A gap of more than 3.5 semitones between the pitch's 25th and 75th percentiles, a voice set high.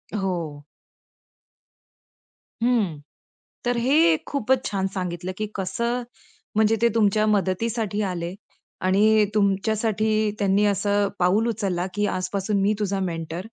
No: average, 2.7 semitones; high, 205 Hz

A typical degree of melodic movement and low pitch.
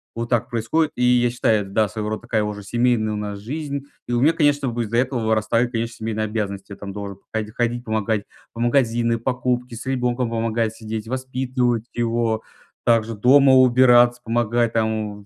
No: narrow, 2.1 semitones; low, 115 Hz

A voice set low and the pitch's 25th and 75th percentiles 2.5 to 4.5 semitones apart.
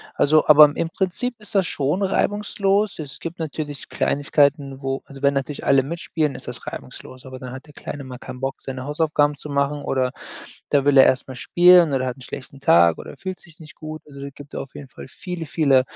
No: medium, 145 Hz; average, 3.3 semitones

